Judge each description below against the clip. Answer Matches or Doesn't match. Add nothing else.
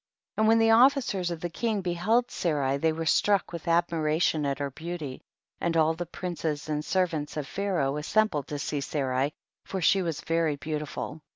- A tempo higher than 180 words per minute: Matches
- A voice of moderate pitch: Matches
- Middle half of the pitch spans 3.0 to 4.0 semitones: Matches